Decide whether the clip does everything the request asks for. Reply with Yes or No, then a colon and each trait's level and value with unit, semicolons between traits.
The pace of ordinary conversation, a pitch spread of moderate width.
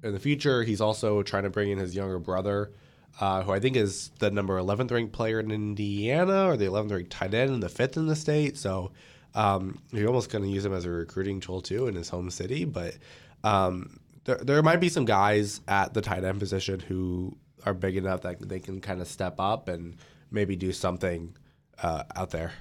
No: fast, 225 wpm; average, 3.6 semitones